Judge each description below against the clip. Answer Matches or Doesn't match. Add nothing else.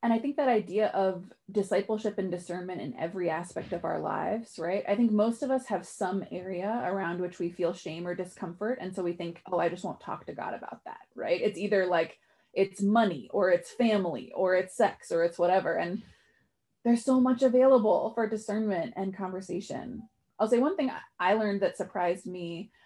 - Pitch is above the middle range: Matches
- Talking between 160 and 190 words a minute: Doesn't match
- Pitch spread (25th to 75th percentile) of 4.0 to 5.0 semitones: Doesn't match